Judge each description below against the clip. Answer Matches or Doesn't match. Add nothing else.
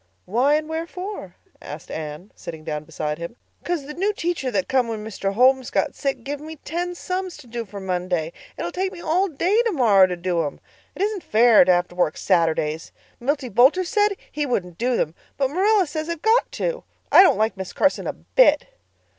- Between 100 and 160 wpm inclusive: Doesn't match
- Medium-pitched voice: Doesn't match